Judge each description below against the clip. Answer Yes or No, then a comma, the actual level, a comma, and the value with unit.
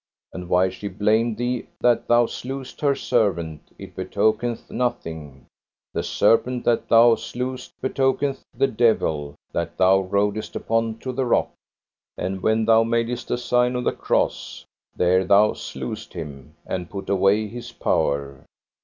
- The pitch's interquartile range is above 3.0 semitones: Yes, average, 4.7 semitones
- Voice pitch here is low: Yes, low, 110 Hz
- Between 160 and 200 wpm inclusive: No, average, 145 wpm